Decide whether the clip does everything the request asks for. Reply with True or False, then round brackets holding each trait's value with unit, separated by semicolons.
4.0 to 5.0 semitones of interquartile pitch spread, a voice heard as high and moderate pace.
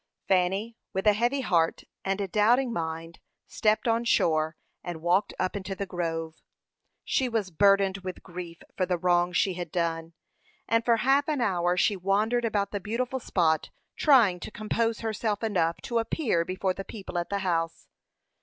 True (4.4 semitones; 195 Hz; 175 wpm)